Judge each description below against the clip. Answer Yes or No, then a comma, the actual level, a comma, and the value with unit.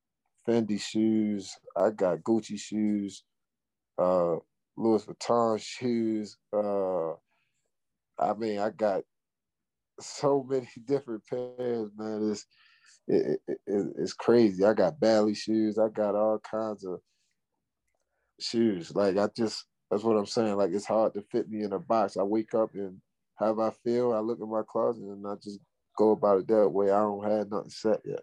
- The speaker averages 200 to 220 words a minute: No, average, 170 wpm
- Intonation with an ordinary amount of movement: No, narrow, 1.6 semitones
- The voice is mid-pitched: No, low, 110 Hz